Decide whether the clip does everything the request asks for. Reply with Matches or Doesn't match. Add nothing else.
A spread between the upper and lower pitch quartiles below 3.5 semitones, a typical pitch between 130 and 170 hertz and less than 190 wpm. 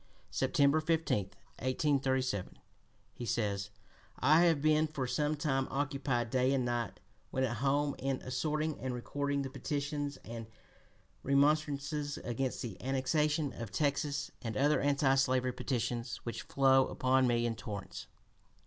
Matches